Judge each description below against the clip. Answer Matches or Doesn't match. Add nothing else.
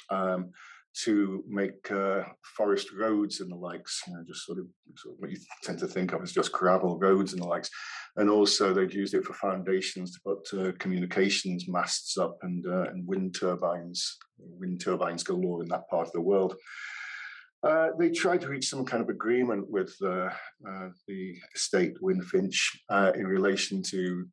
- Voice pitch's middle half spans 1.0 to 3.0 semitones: Matches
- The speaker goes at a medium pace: Matches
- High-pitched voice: Doesn't match